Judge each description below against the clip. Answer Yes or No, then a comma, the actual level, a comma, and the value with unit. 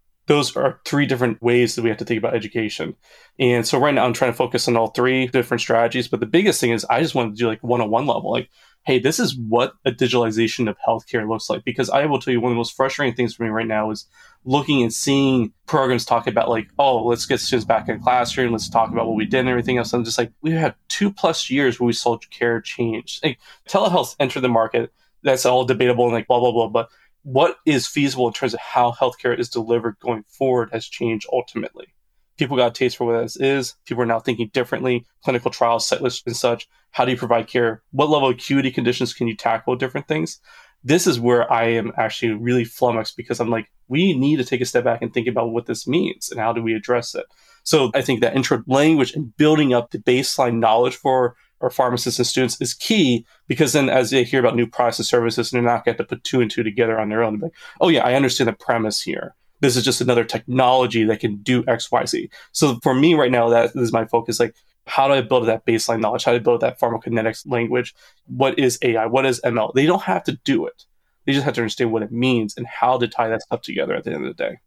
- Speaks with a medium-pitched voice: No, low, 120 Hz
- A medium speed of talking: No, fast, 250 wpm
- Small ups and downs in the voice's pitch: Yes, narrow, 1.9 semitones